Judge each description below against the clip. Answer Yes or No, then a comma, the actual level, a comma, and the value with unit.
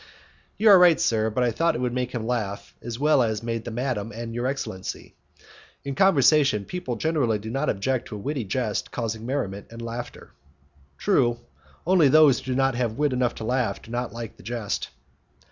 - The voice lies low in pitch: Yes, low, 120 Hz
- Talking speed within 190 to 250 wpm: Yes, average, 195 wpm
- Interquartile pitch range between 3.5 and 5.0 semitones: No, average, 3.1 semitones